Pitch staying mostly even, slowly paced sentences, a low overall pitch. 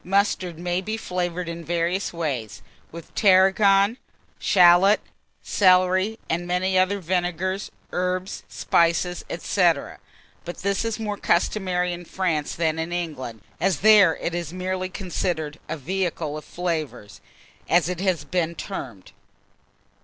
No: narrow, 2.1 semitones; slow, 130 wpm; medium, 180 Hz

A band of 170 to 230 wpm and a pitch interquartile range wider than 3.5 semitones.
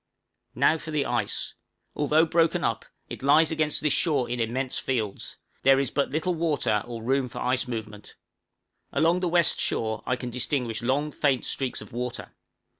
Yes: average, 175 wpm; average, 4.1 semitones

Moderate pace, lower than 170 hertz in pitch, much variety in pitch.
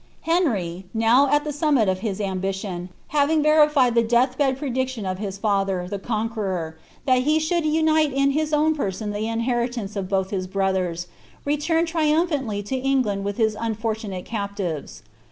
No: average, 160 wpm; high, 230 Hz; wide, 6.8 semitones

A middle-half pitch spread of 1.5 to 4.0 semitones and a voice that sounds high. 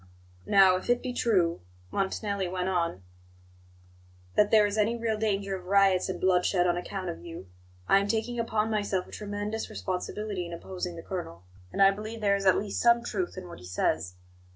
Yes: average, 2.9 semitones; high, 195 Hz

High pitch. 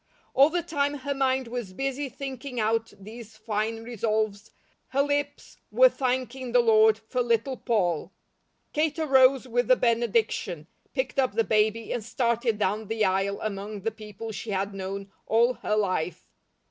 Yes: high, 230 Hz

